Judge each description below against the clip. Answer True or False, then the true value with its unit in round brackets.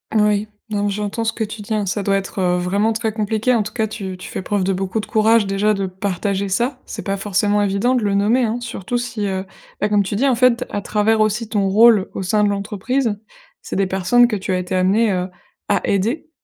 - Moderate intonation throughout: False (2.2 semitones)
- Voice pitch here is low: False (205 Hz)